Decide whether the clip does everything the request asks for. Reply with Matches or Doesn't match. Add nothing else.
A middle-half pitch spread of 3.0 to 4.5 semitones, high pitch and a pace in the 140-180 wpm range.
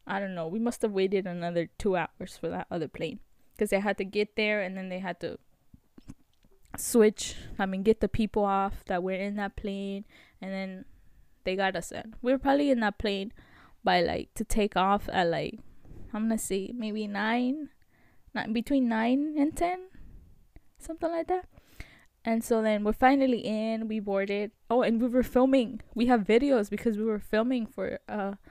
Doesn't match